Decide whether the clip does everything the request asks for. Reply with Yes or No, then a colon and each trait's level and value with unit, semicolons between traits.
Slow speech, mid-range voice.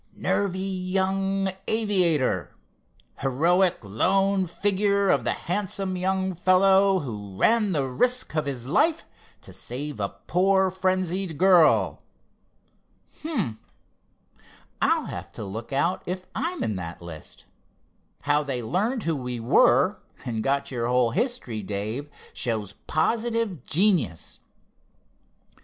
Yes: slow, 115 wpm; medium, 180 Hz